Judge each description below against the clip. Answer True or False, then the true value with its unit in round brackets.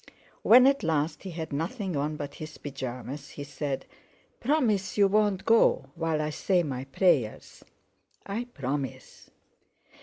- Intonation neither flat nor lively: False (6.0 semitones)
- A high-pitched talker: False (160 Hz)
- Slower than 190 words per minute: True (140 wpm)